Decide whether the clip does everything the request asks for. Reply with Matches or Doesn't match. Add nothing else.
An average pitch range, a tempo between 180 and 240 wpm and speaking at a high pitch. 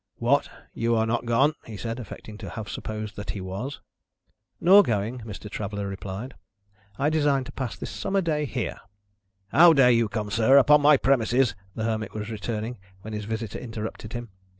Doesn't match